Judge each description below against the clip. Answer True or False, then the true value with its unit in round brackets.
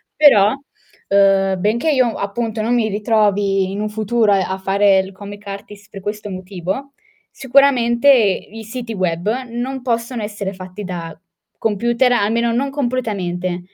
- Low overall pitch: False (210 Hz)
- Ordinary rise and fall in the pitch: True (3.5 semitones)